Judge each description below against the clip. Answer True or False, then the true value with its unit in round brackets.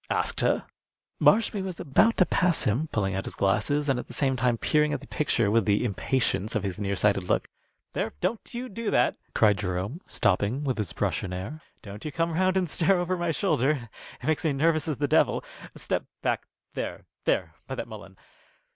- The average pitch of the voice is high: False (135 Hz)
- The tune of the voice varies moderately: False (8.1 semitones)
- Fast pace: True (210 wpm)